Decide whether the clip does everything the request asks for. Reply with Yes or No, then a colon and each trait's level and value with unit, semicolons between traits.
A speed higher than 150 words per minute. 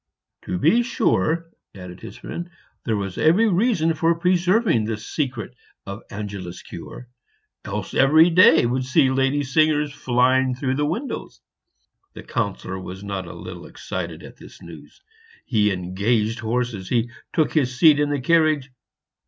No: average, 145 wpm